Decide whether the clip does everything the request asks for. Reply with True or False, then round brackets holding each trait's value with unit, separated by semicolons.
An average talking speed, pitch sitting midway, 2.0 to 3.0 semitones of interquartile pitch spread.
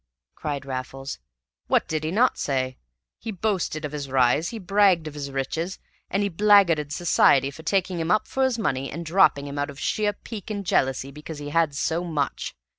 False (195 wpm; 160 Hz; 5.6 semitones)